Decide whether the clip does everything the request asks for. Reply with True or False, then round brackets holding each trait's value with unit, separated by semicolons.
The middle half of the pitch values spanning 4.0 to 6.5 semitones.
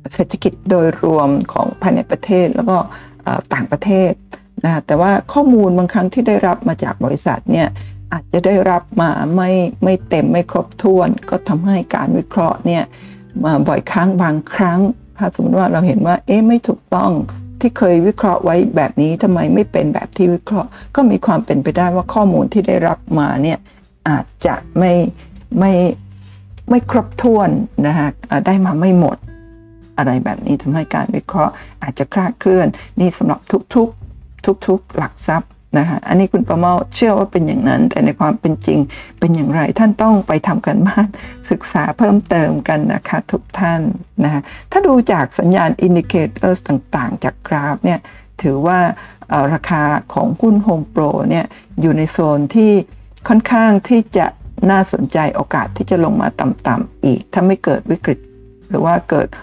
True (4.6 semitones)